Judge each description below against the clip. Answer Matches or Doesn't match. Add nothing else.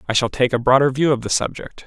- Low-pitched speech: Matches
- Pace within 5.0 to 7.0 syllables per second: Matches